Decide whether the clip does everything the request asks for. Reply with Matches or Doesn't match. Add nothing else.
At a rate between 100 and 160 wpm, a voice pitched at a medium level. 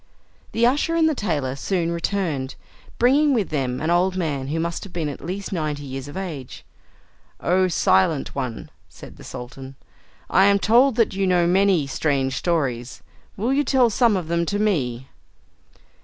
Doesn't match